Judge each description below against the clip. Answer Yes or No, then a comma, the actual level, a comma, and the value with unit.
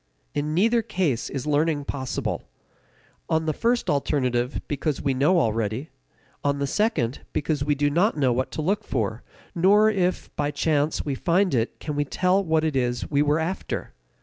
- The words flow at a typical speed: Yes, average, 180 wpm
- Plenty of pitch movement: No, average, 4.6 semitones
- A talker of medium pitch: Yes, medium, 150 Hz